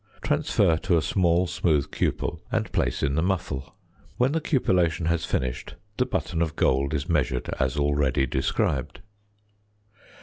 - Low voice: Yes, very low, 80 Hz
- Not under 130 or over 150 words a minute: Yes, average, 145 wpm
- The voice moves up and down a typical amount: Yes, average, 4.1 semitones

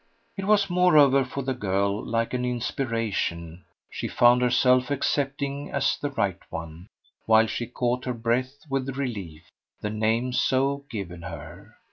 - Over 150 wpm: No, average, 145 wpm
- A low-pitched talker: Yes, low, 125 Hz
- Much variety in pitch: No, average, 4.1 semitones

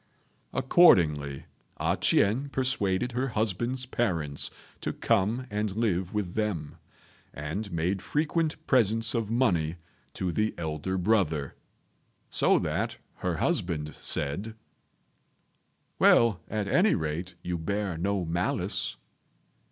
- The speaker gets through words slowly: Yes, slow, 110 wpm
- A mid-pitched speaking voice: No, low, 100 Hz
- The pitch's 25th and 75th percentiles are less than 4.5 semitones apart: No, wide, 5.4 semitones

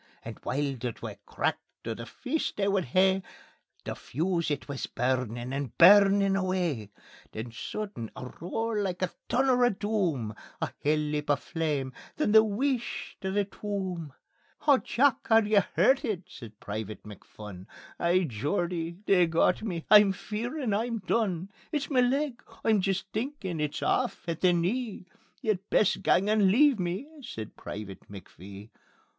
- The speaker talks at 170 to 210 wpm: No, average, 155 wpm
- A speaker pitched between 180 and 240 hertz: Yes, medium, 185 Hz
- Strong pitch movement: Yes, wide, 7.0 semitones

